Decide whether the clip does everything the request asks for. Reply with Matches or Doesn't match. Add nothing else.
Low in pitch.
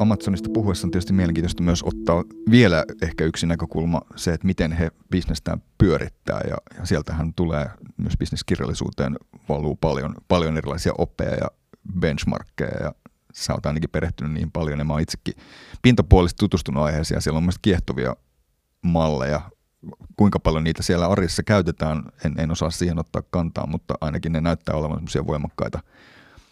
Matches